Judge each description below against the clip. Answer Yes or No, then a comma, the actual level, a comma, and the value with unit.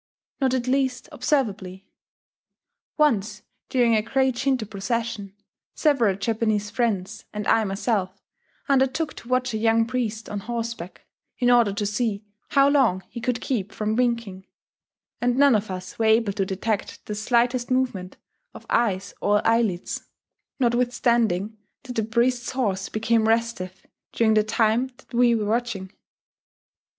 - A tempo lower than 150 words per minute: Yes, average, 140 wpm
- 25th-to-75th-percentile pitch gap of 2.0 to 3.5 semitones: Yes, average, 3.1 semitones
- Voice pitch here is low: No, high, 225 Hz